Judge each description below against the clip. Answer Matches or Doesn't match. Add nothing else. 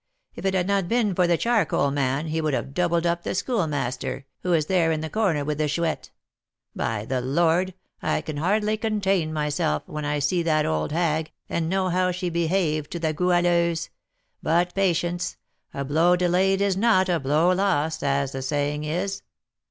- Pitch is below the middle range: Doesn't match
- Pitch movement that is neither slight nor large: Matches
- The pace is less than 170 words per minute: Doesn't match